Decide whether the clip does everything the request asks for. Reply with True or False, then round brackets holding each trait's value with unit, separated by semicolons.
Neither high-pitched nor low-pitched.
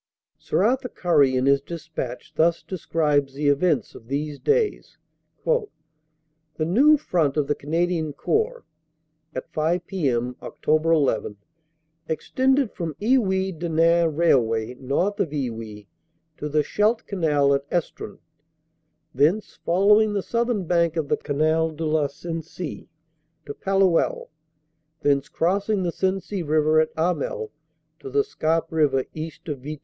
True (160 Hz)